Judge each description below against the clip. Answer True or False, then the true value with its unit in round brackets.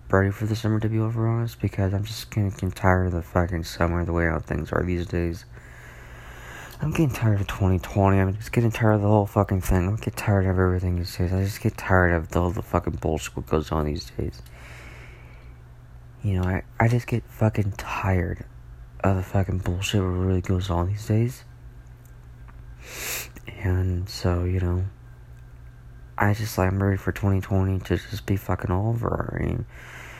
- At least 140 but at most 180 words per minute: False (200 wpm)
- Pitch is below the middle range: True (95 Hz)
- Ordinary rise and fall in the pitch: True (4.0 semitones)